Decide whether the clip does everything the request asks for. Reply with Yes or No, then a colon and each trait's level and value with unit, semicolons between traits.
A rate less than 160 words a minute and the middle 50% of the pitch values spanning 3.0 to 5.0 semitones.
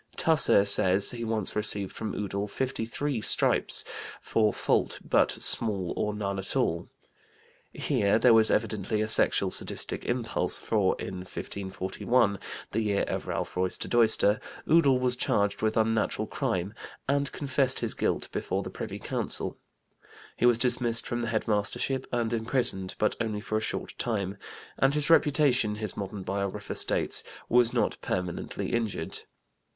Yes: average, 150 wpm; average, 3.3 semitones